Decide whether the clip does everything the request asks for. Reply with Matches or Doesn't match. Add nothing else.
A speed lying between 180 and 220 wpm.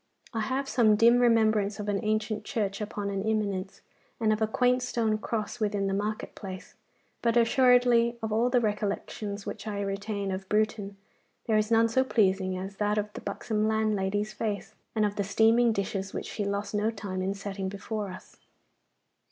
Matches